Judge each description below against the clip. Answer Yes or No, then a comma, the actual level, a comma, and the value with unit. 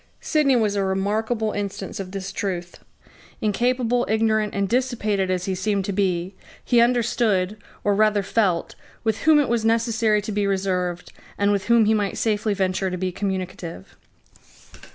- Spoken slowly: No, average, 160 wpm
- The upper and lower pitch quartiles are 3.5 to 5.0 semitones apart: No, average, 2.8 semitones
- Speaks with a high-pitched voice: Yes, high, 205 Hz